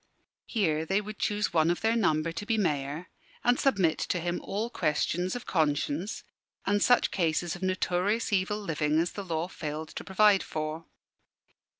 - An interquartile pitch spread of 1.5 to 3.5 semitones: No, average, 4.6 semitones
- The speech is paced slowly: No, average, 170 wpm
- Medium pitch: Yes, medium, 180 Hz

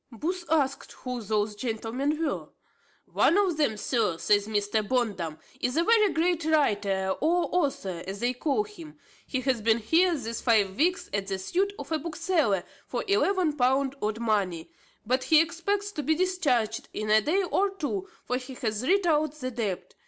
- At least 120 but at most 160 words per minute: No, average, 180 wpm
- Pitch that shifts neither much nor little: No, wide, 7.7 semitones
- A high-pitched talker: Yes, very high, 265 Hz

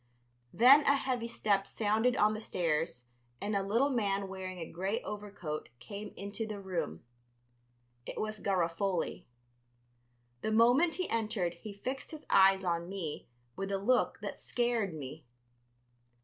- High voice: Yes, high, 200 Hz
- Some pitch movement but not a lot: Yes, average, 3.9 semitones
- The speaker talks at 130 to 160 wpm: Yes, average, 145 wpm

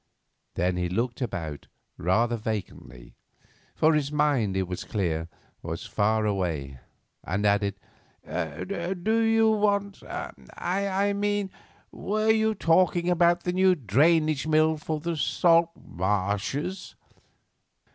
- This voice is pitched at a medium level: Yes, medium, 150 Hz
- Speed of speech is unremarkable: No, slow, 115 wpm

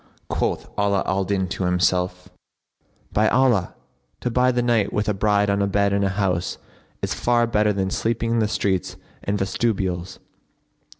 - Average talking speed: Yes, average, 170 wpm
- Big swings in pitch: No, average, 2.7 semitones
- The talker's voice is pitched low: Yes, low, 100 Hz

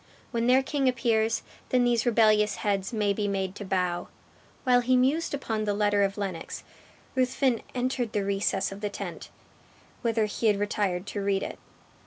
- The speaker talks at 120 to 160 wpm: No, average, 175 wpm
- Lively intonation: No, average, 3.6 semitones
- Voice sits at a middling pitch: No, high, 215 Hz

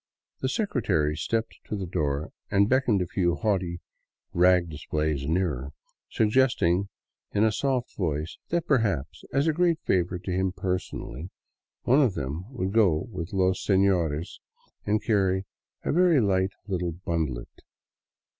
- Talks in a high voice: No, very low, 95 Hz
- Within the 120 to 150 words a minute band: Yes, average, 145 wpm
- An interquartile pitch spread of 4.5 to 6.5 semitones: Yes, average, 4.8 semitones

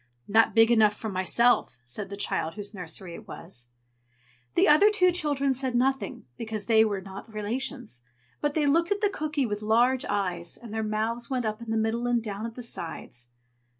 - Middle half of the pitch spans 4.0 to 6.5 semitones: Yes, average, 4.3 semitones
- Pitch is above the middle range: Yes, high, 225 Hz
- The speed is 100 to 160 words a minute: No, average, 195 wpm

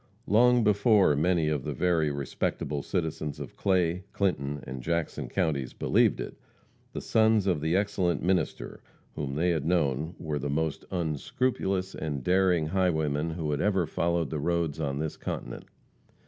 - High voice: No, very low, 80 Hz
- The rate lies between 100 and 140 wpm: No, average, 155 wpm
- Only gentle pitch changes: No, average, 4.0 semitones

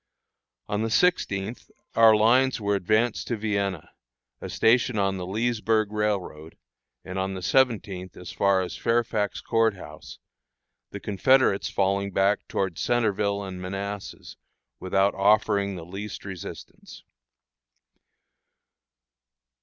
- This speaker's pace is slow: Yes, slow, 115 wpm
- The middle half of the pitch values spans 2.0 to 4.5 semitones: Yes, narrow, 2.5 semitones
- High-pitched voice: No, low, 100 Hz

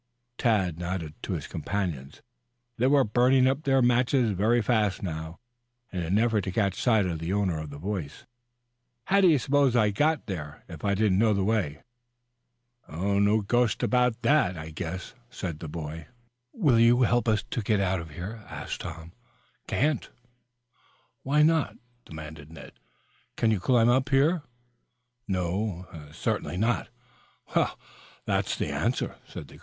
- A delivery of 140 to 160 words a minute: Yes, average, 155 wpm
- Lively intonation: Yes, wide, 6.0 semitones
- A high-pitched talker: No, low, 105 Hz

